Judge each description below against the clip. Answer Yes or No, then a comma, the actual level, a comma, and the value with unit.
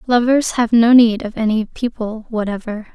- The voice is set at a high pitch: Yes, high, 230 Hz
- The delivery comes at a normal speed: Yes, average, 165 wpm